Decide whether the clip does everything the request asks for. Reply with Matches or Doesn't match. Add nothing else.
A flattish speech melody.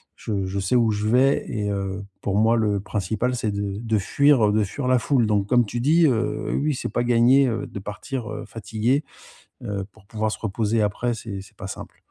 Doesn't match